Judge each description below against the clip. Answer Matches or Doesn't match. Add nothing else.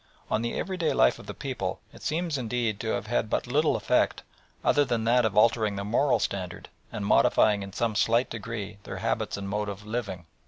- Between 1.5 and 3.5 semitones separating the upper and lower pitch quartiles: Matches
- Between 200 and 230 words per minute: Matches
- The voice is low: Matches